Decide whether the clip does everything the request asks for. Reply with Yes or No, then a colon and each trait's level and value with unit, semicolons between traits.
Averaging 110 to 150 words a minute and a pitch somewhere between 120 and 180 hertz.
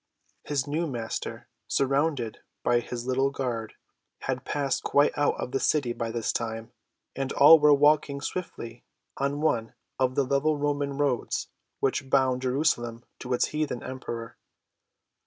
Yes: average, 145 wpm; low, 135 Hz